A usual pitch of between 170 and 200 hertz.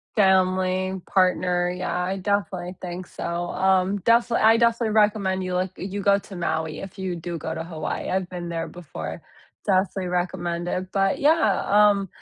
Yes: medium, 185 Hz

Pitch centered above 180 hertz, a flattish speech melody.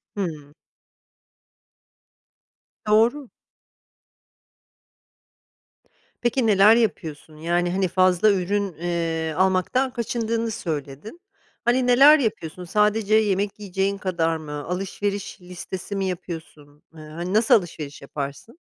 No: high, 190 Hz; average, 4.8 semitones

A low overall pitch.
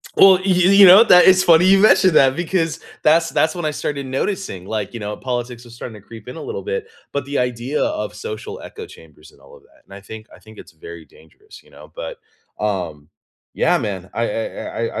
No: medium, 150 Hz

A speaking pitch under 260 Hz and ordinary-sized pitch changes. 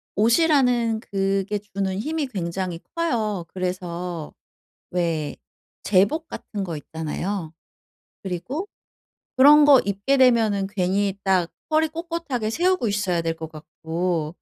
No: high, 200 Hz; wide, 6.0 semitones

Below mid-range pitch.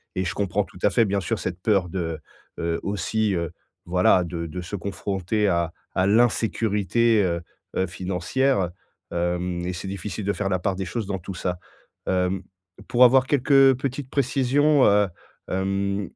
Yes: very low, 95 Hz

